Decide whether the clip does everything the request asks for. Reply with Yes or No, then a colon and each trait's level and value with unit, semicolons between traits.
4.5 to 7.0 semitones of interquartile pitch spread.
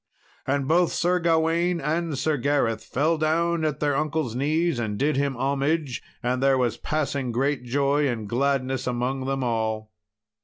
No: average, 3.7 semitones